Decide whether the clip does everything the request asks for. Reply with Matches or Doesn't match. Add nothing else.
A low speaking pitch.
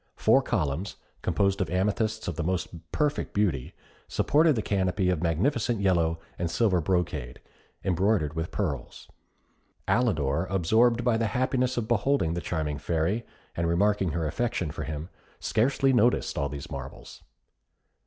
Matches